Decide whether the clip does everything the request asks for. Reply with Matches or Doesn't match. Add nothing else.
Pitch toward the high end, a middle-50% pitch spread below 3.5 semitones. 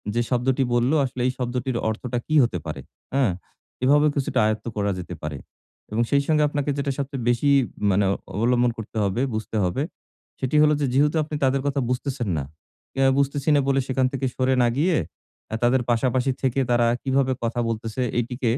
Doesn't match